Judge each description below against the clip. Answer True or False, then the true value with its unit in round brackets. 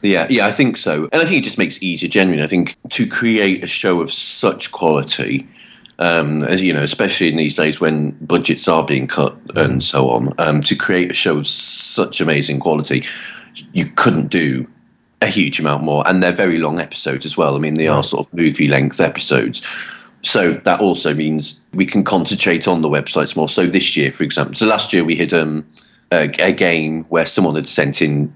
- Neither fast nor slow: False (215 wpm)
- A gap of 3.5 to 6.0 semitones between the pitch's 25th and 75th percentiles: False (2.9 semitones)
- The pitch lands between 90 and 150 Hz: False (80 Hz)